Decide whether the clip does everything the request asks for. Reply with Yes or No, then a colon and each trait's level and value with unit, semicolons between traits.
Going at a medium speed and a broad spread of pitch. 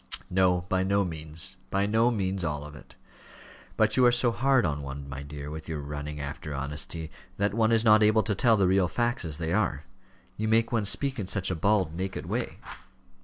No: fast, 215 wpm; wide, 6.1 semitones